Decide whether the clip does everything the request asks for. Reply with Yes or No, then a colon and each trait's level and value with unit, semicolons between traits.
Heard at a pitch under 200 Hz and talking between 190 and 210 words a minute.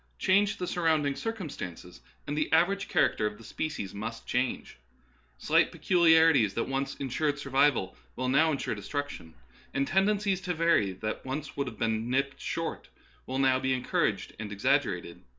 No: medium, 140 Hz; average, 160 wpm